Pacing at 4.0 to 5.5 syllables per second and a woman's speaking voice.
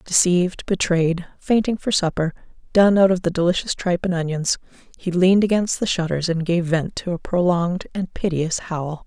Yes: 5.2 syllables/s; female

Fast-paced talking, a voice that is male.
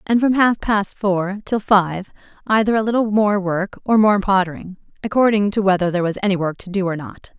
No: fast, 210 wpm; female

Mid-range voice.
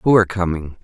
No: very low, 95 Hz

